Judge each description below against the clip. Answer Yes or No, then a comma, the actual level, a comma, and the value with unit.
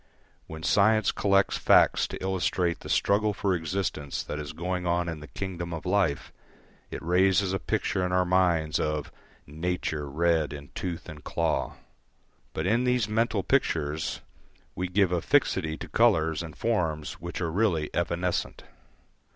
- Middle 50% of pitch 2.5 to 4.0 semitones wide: Yes, average, 3.4 semitones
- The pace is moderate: Yes, average, 155 wpm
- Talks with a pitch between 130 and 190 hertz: No, very low, 90 Hz